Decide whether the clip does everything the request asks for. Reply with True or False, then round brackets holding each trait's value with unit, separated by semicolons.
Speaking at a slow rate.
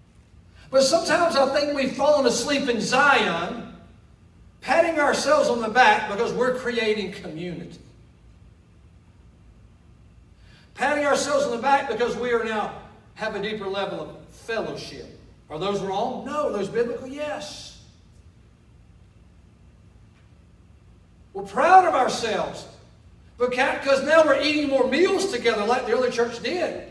True (125 wpm)